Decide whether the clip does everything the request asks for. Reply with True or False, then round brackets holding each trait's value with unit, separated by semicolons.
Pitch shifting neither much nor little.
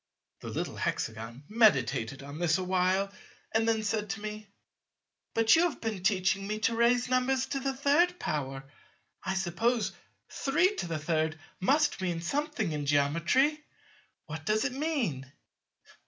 False (7.9 semitones)